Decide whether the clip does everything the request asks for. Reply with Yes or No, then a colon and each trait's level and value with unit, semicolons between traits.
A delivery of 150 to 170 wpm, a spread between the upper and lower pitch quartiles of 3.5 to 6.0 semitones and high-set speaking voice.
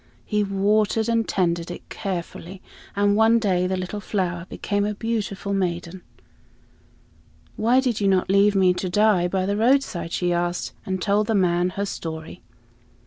No: average, 165 wpm; average, 2.8 semitones; high, 195 Hz